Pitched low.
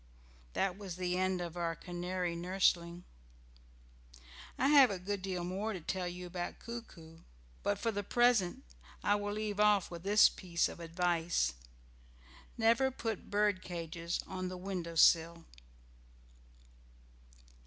No: medium, 185 Hz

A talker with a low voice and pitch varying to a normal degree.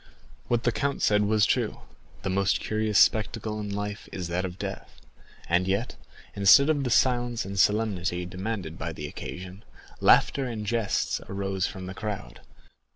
Yes: low, 100 Hz; average, 3.1 semitones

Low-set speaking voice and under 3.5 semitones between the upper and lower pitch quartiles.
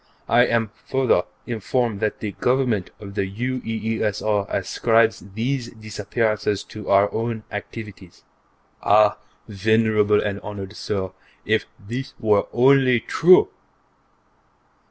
Yes: low, 110 Hz; narrow, 2.5 semitones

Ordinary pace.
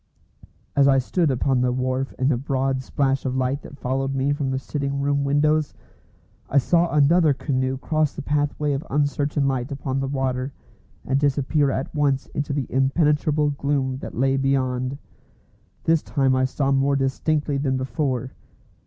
Yes: average, 165 wpm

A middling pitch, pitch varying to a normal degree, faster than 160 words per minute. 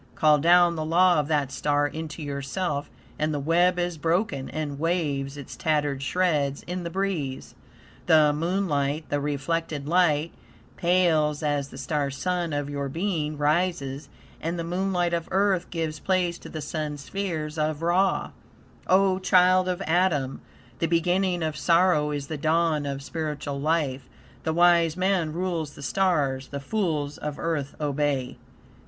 No: medium, 155 Hz; average, 3.3 semitones; average, 155 wpm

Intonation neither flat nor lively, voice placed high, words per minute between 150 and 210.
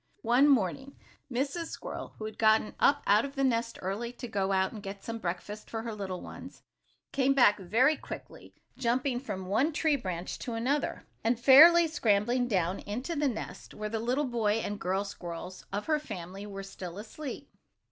Yes: average, 5.0 semitones; high, 225 Hz; average, 185 wpm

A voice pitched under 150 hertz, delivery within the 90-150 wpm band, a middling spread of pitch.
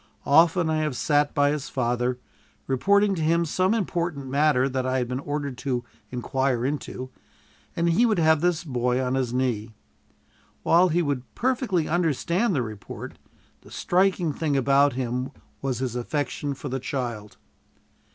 No: medium, 140 Hz; average, 160 wpm; average, 4.7 semitones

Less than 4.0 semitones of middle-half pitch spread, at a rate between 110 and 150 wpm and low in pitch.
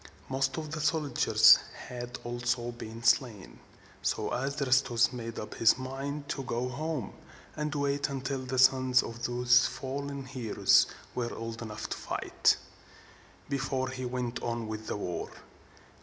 Yes: narrow, 2.5 semitones; average, 140 wpm; low, 125 Hz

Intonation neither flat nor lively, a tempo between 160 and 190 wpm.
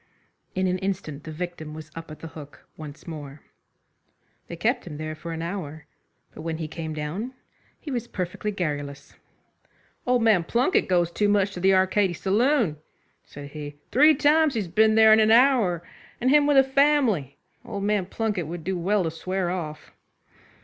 No: wide, 5.8 semitones; average, 180 wpm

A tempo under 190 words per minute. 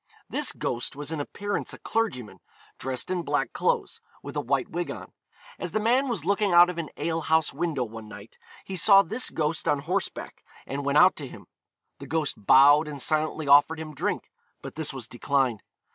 No: average, 195 wpm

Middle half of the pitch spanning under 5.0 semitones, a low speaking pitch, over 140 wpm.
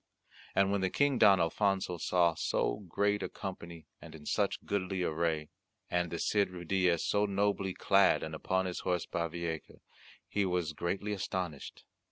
Yes: narrow, 2.6 semitones; very low, 90 Hz; average, 160 wpm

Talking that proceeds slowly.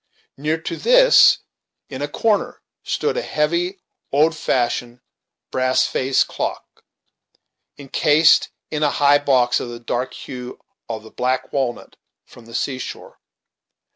Yes: slow, 130 wpm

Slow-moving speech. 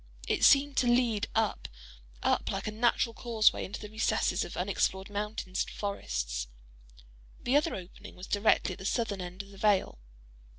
No: average, 170 wpm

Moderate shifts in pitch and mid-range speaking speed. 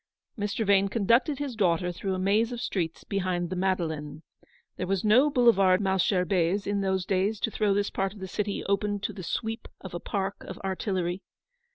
No: narrow, 2.2 semitones; average, 190 wpm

